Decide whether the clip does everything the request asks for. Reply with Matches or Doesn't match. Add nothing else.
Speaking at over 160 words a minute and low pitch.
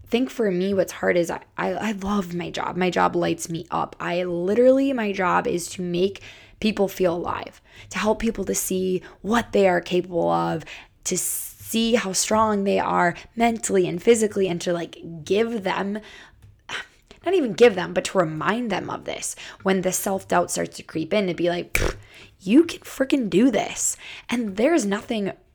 Doesn't match